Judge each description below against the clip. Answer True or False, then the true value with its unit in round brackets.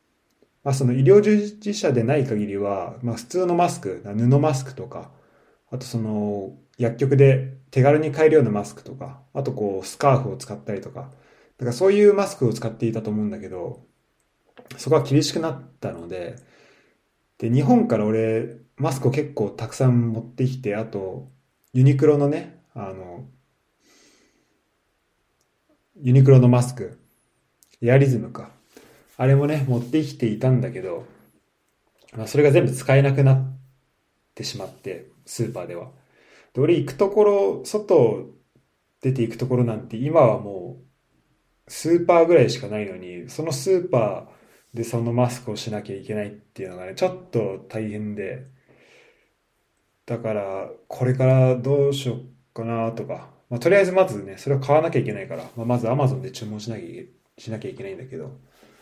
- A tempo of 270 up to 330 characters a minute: True (320 characters per minute)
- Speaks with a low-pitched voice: True (125 Hz)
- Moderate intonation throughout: True (3.8 semitones)